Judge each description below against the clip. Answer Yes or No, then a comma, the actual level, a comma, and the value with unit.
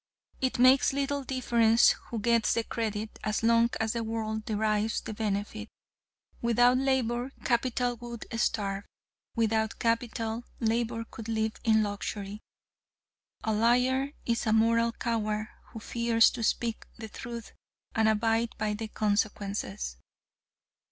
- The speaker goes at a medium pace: No, slow, 130 wpm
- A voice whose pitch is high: Yes, high, 225 Hz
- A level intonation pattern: Yes, narrow, 1.5 semitones